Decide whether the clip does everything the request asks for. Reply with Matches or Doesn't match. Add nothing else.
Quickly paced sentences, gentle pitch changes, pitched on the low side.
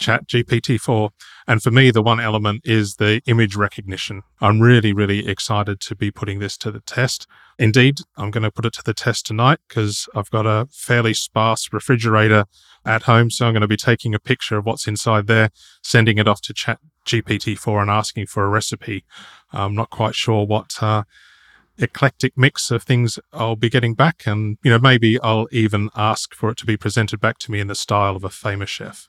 Matches